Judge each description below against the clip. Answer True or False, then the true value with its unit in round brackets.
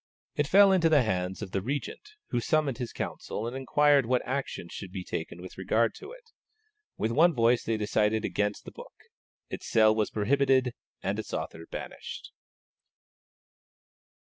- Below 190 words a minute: True (165 wpm)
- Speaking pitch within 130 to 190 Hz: False (120 Hz)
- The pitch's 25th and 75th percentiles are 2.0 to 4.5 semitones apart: False (5.3 semitones)